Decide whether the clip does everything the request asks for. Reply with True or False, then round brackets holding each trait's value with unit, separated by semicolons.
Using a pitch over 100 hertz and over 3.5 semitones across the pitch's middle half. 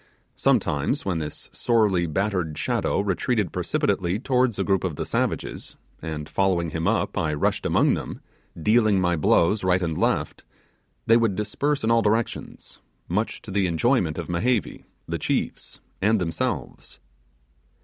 False (95 Hz; 4.6 semitones)